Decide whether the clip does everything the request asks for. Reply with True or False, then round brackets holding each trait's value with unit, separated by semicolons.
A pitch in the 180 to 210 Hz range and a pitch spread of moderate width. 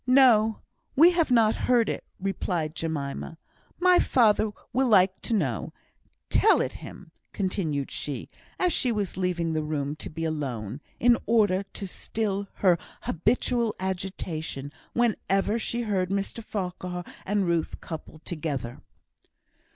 False (190 Hz; 5.7 semitones)